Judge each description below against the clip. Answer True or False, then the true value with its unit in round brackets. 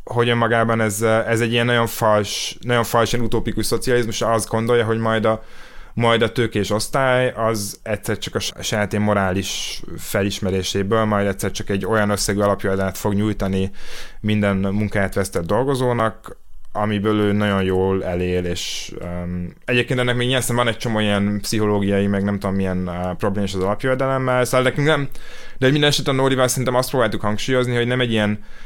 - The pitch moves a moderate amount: True (3.2 semitones)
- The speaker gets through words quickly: True (170 wpm)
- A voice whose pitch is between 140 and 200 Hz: False (110 Hz)